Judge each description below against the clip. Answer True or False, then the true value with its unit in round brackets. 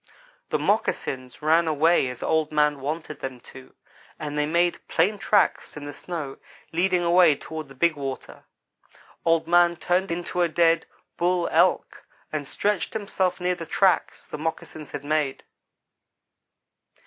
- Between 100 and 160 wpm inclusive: True (150 wpm)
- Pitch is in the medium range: True (160 Hz)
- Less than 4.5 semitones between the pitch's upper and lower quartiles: True (2.9 semitones)